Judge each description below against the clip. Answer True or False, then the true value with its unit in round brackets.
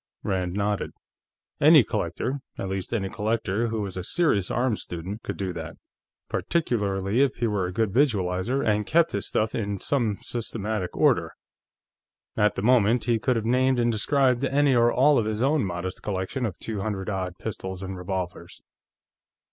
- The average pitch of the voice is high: False (105 Hz)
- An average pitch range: True (4.1 semitones)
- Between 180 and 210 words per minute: False (170 wpm)